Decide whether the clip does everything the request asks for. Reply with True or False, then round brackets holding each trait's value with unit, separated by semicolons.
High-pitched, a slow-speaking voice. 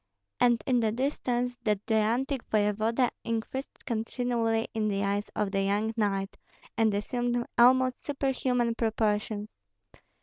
True (225 Hz; 125 wpm)